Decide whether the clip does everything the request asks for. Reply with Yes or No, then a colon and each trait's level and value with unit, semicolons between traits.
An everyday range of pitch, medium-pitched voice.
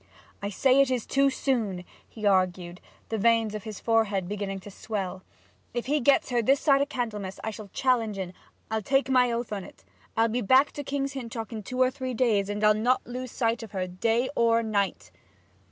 No: average, 3.8 semitones; high, 225 Hz